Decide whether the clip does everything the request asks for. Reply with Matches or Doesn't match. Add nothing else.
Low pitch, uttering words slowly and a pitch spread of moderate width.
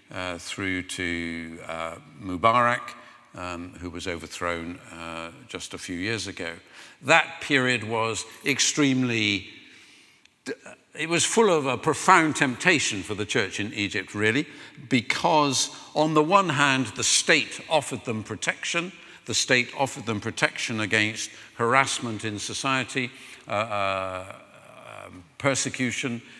Doesn't match